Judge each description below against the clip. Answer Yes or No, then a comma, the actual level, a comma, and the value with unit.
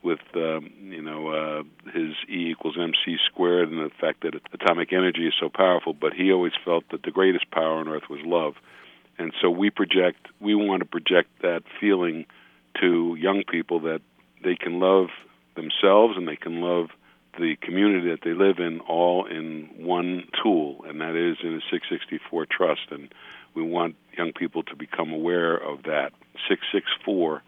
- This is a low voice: Yes, very low, 85 Hz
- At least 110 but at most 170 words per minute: No, average, 180 wpm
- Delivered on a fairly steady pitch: Yes, narrow, 2.0 semitones